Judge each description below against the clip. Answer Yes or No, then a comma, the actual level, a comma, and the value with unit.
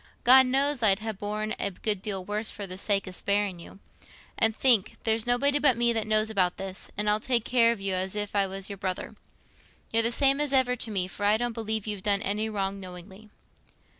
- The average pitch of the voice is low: No, high, 210 Hz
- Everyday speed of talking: No, fast, 225 wpm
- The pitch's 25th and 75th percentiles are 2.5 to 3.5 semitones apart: Yes, average, 3.1 semitones